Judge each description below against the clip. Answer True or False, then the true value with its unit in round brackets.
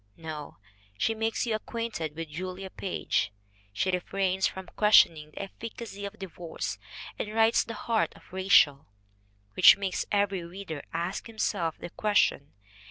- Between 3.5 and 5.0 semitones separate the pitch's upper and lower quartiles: True (4.3 semitones)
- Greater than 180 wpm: False (140 wpm)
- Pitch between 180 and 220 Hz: True (190 Hz)